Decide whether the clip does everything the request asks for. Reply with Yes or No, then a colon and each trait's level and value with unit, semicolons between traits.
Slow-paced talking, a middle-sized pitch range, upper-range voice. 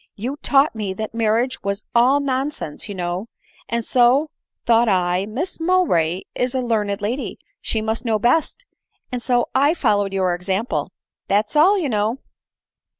No: average, 165 wpm; average, 4.7 semitones; high, 230 Hz